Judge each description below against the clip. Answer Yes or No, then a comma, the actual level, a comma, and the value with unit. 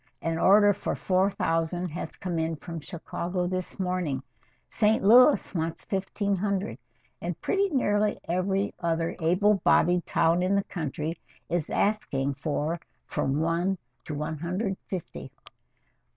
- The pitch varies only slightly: No, average, 3.3 semitones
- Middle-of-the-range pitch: Yes, medium, 180 Hz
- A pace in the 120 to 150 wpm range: Yes, average, 140 wpm